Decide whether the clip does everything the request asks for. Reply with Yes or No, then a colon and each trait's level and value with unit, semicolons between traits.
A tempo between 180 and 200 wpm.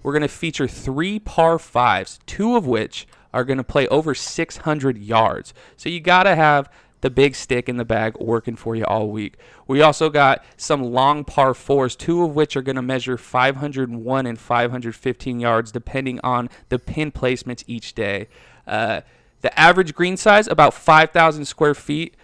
No: average, 170 wpm